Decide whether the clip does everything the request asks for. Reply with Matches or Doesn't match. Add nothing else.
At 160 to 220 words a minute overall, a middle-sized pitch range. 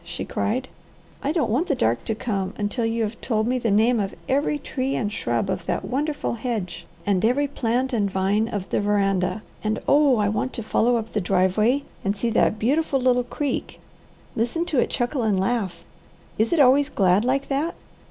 Matches